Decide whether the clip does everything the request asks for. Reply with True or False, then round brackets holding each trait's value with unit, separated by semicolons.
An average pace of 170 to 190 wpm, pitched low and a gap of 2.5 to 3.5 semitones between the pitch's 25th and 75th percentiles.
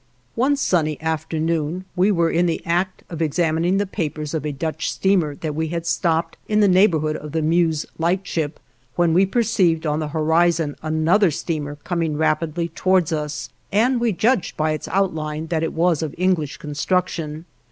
False (175 wpm; 165 Hz; 2.8 semitones)